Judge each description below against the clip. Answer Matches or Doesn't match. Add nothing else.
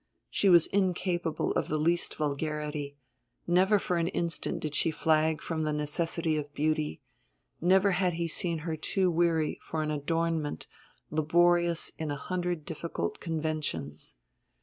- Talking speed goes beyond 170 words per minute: Doesn't match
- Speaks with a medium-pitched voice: Matches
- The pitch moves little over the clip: Matches